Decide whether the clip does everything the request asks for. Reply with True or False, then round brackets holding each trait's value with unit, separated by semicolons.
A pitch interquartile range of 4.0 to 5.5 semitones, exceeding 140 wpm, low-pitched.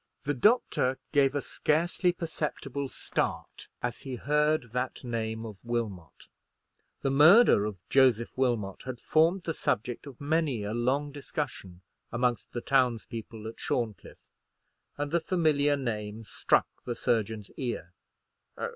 False (4.4 semitones; 135 wpm; 125 Hz)